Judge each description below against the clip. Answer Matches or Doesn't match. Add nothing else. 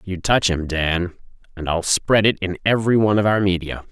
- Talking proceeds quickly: Matches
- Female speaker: Doesn't match